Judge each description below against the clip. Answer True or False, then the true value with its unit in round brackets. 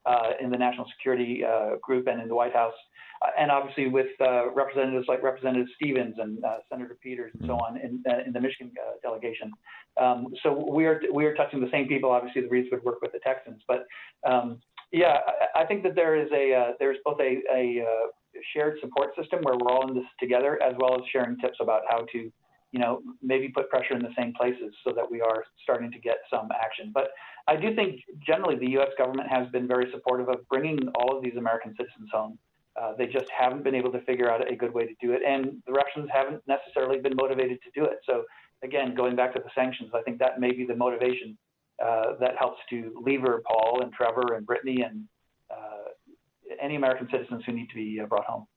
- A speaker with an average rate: False (225 wpm)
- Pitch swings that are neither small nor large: False (2.0 semitones)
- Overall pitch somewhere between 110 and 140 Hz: True (125 Hz)